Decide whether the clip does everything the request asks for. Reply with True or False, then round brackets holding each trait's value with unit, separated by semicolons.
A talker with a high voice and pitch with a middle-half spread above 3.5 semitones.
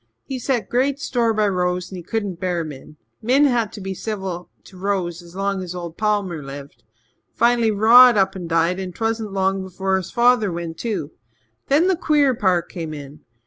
True (195 Hz; 4.6 semitones)